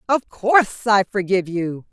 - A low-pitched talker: No, high, 205 Hz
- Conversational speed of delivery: Yes, average, 155 wpm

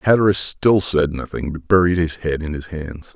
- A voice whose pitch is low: Yes, very low, 85 Hz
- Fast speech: Yes, fast, 210 wpm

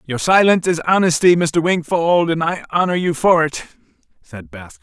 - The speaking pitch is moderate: Yes, medium, 160 Hz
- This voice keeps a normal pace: Yes, average, 175 wpm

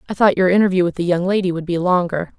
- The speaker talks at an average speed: No, fast, 275 wpm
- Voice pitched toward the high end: No, medium, 180 Hz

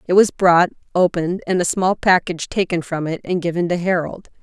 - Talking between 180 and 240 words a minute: Yes, fast, 205 wpm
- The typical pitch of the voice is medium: Yes, medium, 175 Hz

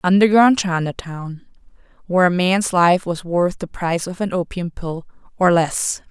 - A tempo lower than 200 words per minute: Yes, average, 140 wpm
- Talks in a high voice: No, medium, 180 Hz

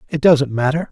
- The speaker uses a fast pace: No, average, 195 wpm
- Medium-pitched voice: Yes, medium, 145 Hz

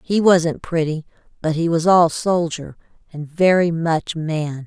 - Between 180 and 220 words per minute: No, average, 155 wpm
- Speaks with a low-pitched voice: No, medium, 165 Hz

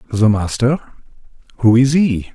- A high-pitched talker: No, low, 120 Hz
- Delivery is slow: Yes, slow, 100 wpm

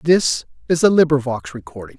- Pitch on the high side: No, low, 135 Hz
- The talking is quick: No, average, 150 wpm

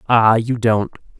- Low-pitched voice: Yes, low, 115 Hz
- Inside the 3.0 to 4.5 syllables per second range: Yes, 4.0 syllables/s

